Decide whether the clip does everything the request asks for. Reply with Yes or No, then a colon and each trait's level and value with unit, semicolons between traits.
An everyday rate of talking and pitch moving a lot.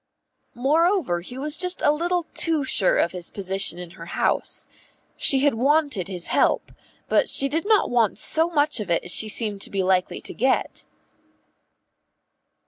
Yes: average, 170 wpm; wide, 8.5 semitones